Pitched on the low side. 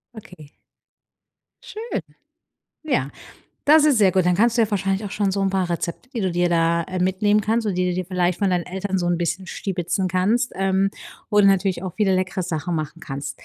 No: medium, 185 Hz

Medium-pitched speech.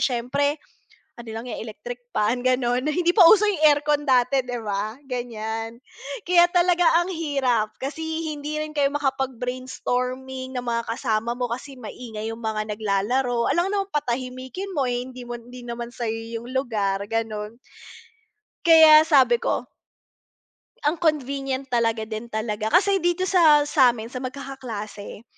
No: very high, 255 Hz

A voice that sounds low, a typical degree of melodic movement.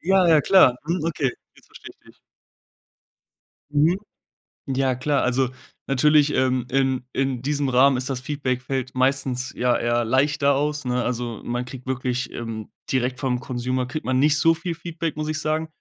Yes: low, 130 Hz; average, 3.0 semitones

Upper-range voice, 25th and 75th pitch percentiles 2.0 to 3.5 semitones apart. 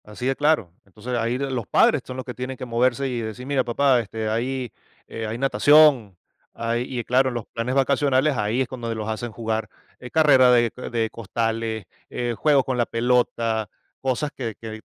No: low, 120 Hz; narrow, 2.6 semitones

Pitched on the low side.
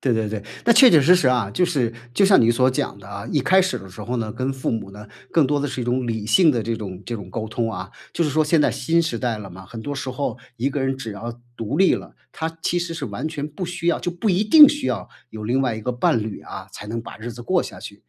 Yes: low, 125 Hz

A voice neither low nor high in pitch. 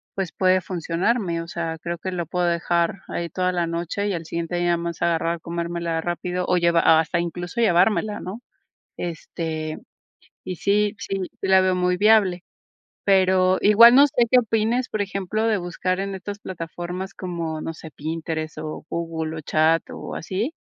Yes: medium, 175 Hz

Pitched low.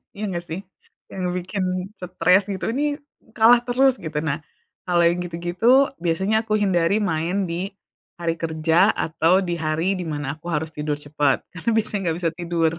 No: medium, 175 Hz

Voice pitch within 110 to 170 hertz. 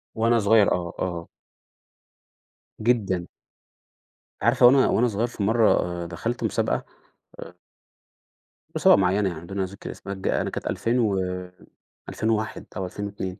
No: low, 100 Hz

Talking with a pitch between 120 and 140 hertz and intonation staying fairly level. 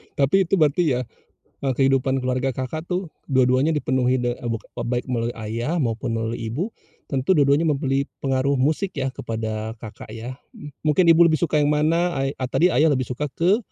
No: low, 135 Hz; average, 4.0 semitones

